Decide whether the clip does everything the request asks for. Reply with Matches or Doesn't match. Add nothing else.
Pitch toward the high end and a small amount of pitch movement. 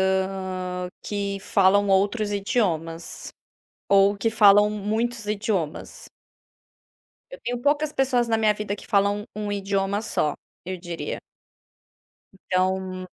Matches